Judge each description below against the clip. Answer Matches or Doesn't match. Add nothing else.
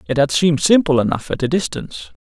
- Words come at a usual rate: Doesn't match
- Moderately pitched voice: Matches